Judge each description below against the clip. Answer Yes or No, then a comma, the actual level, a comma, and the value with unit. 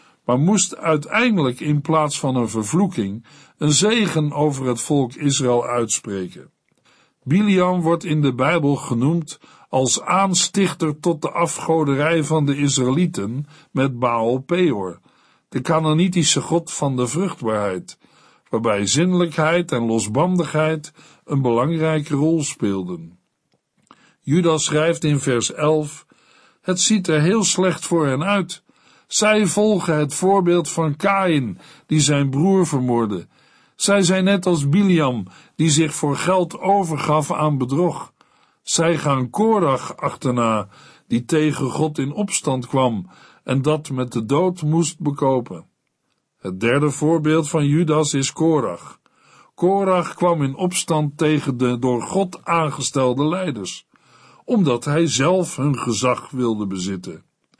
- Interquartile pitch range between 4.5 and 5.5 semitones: Yes, average, 4.8 semitones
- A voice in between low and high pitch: Yes, medium, 155 Hz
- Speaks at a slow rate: Yes, slow, 125 wpm